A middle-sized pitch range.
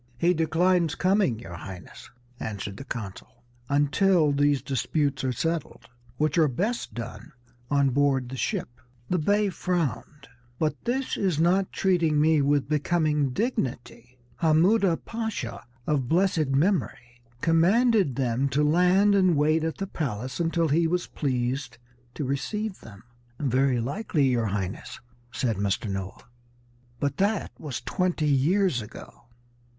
No: wide, 5.9 semitones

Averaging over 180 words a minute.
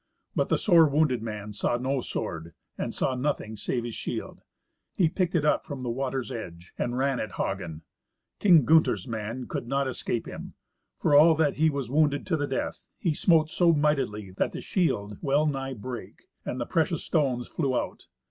Yes: average, 190 wpm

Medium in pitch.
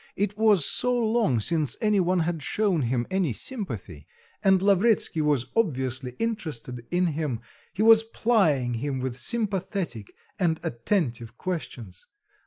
Yes: medium, 165 Hz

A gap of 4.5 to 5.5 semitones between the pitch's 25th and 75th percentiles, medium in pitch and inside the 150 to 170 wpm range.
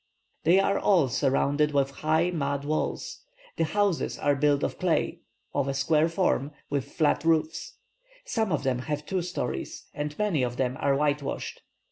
No: average, 2.9 semitones; medium, 150 Hz; average, 165 wpm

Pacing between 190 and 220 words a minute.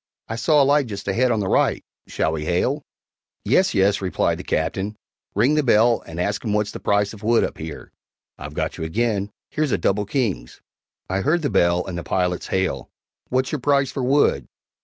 Yes: average, 200 wpm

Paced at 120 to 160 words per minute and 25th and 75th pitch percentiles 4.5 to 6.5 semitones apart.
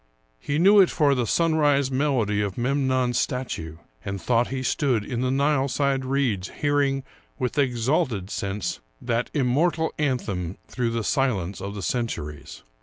Yes: average, 150 wpm; average, 5.0 semitones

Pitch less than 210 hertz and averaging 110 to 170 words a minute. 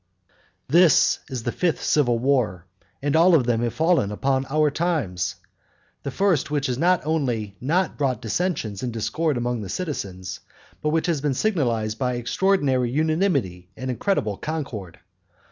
Yes: low, 135 Hz; average, 160 wpm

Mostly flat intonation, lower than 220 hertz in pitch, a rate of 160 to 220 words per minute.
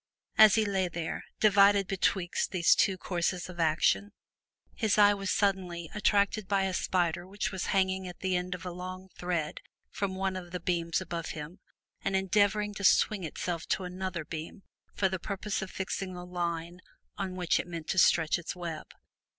Yes: narrow, 2.1 semitones; medium, 185 Hz; average, 185 wpm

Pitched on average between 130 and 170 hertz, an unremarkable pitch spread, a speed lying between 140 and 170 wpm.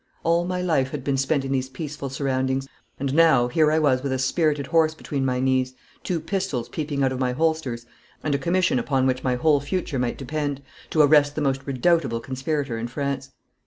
No: medium, 140 Hz; average, 3.0 semitones; fast, 205 wpm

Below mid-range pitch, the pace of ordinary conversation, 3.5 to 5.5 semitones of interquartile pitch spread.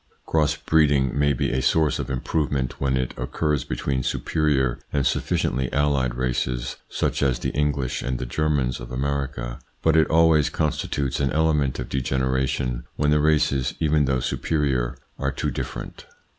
No: very low, 70 Hz; average, 155 wpm; average, 2.7 semitones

